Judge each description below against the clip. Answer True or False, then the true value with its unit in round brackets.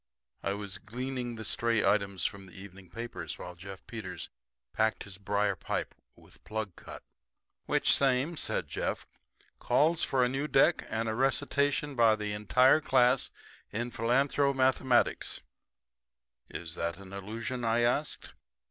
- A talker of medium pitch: False (115 Hz)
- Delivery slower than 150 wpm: True (140 wpm)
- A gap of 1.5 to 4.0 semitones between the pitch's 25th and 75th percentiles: False (4.6 semitones)